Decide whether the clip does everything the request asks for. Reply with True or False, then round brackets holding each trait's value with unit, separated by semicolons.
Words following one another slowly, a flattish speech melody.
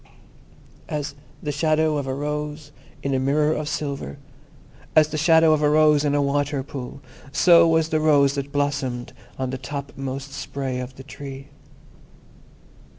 False (155 wpm; 2.0 semitones)